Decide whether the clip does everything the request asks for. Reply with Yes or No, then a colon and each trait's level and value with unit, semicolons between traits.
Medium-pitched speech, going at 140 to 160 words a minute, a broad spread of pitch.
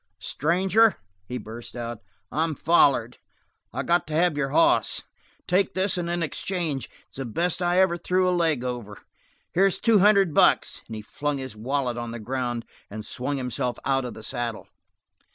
No: medium, 145 Hz; average, 175 wpm; wide, 6.5 semitones